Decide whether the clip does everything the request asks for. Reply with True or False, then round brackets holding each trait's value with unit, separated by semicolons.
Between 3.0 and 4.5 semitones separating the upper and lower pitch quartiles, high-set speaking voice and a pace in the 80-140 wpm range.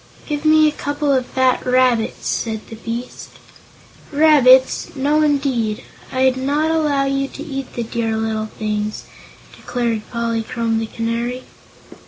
True (3.7 semitones; 255 Hz; 135 wpm)